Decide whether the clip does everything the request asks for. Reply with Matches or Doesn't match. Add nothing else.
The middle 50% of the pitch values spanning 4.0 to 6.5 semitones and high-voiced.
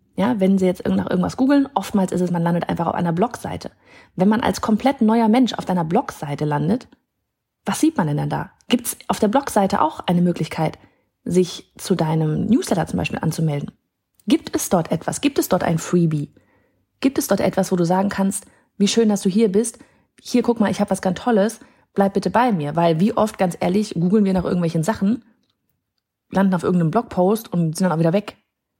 Matches